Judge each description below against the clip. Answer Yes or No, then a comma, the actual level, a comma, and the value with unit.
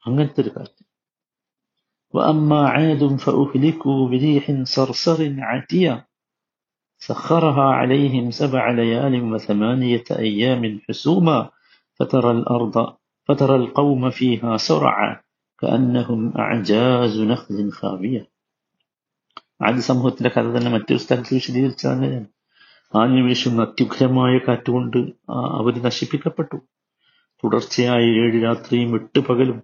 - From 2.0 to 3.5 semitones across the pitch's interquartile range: Yes, average, 2.8 semitones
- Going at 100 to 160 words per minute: No, average, 80 wpm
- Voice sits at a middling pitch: No, low, 125 Hz